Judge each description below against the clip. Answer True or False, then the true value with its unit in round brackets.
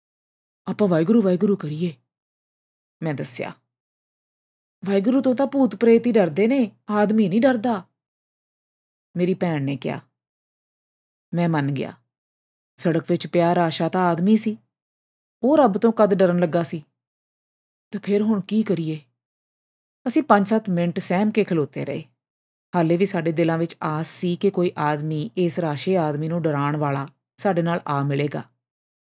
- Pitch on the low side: False (175 Hz)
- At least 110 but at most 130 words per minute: False (140 wpm)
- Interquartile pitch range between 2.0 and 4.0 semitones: False (5.5 semitones)